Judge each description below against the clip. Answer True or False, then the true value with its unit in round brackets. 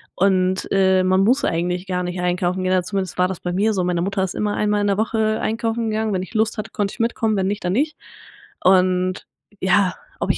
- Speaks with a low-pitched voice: False (190 Hz)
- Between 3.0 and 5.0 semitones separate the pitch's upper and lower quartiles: False (2.6 semitones)